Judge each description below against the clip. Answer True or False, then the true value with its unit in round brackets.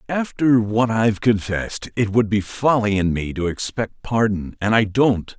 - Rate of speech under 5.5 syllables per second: True (4.5 syllables/s)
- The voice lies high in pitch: False (110 Hz)